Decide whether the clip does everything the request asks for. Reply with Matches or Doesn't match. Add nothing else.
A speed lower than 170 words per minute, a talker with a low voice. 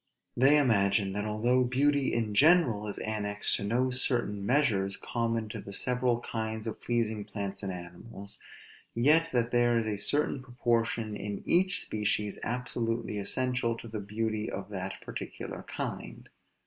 Matches